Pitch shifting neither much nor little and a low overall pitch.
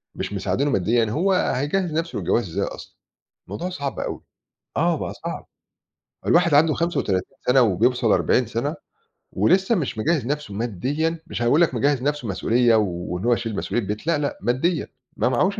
No: wide, 6.1 semitones; low, 130 Hz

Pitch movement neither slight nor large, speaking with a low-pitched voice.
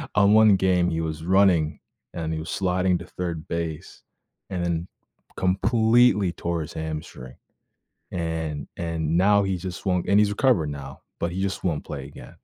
Yes: average, 3.2 semitones; very low, 85 Hz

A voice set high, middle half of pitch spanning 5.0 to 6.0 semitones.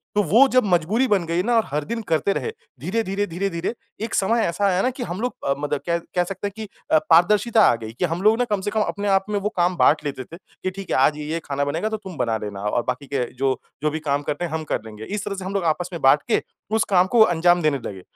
No: medium, 180 Hz; wide, 5.6 semitones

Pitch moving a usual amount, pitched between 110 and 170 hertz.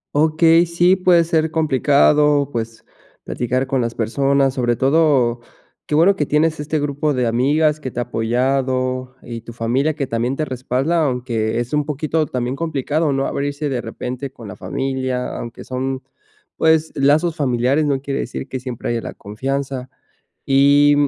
Yes: average, 3.3 semitones; low, 135 Hz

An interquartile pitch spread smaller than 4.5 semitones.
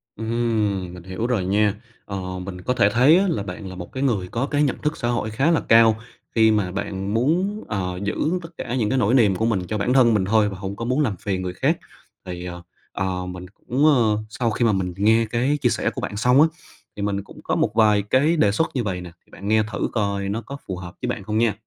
Yes: average, 4.0 semitones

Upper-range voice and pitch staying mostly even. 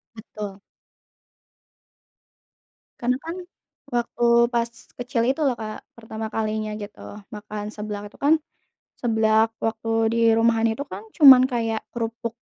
Yes: high, 225 Hz; narrow, 1.9 semitones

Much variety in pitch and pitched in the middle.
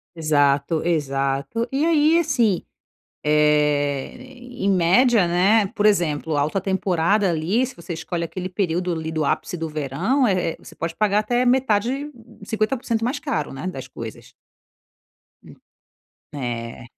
Yes: wide, 6.8 semitones; medium, 180 Hz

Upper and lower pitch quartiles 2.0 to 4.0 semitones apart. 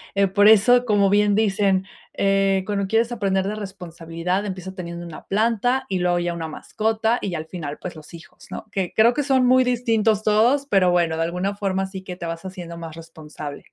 Yes: average, 3.7 semitones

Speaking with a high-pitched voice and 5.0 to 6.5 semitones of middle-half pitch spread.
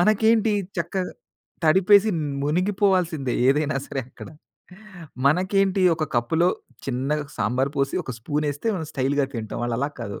No: medium, 155 Hz; wide, 5.6 semitones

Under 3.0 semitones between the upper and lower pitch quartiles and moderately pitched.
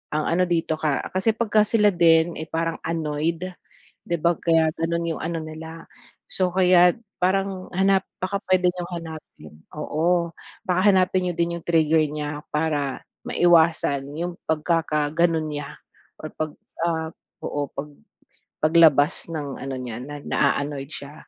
Yes: narrow, 2.6 semitones; medium, 165 Hz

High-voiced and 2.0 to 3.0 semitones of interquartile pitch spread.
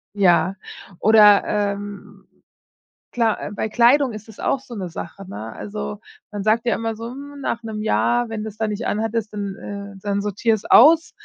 Yes: high, 215 Hz; narrow, 2.5 semitones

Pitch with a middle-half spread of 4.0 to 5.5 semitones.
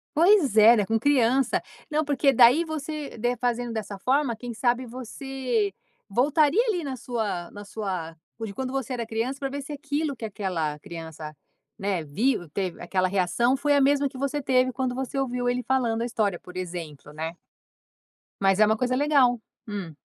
Yes: average, 5.2 semitones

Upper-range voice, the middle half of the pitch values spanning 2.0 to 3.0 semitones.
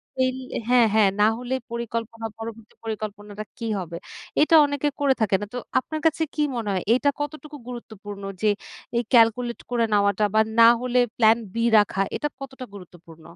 No: high, 230 Hz; average, 3.5 semitones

